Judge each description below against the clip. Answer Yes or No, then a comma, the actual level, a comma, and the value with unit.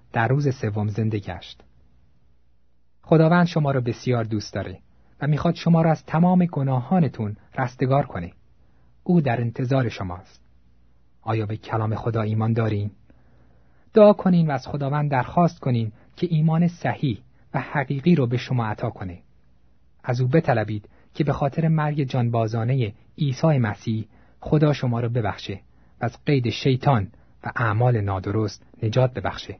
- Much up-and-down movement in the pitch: Yes, wide, 6.2 semitones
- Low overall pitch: Yes, low, 115 Hz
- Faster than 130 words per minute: Yes, average, 140 wpm